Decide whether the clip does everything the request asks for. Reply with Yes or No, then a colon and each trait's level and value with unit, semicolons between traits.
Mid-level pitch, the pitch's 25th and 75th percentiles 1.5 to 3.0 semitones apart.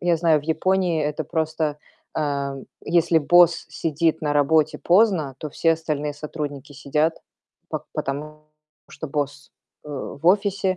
Yes: medium, 155 Hz; narrow, 2.4 semitones